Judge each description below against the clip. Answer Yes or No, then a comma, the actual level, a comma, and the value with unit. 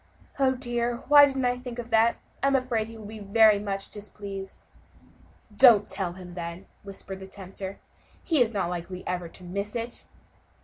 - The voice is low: No, high, 210 Hz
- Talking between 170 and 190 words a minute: Yes, average, 180 wpm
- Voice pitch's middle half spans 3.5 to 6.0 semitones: Yes, average, 3.9 semitones